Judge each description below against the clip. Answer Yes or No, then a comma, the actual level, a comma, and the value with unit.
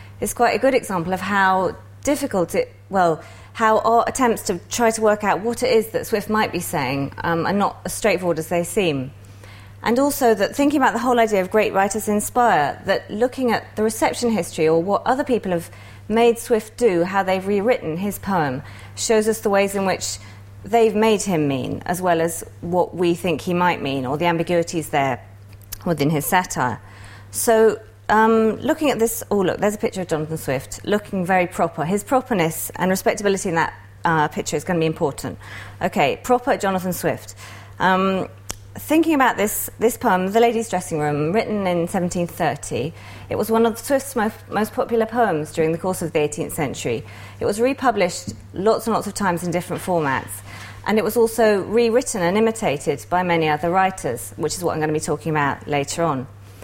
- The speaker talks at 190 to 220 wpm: Yes, average, 195 wpm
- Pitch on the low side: No, medium, 185 Hz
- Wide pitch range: Yes, wide, 6.5 semitones